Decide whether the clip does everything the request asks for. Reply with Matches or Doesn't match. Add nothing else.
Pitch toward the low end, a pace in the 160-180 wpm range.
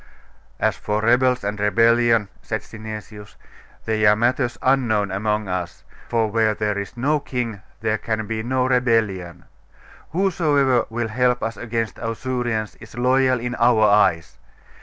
Doesn't match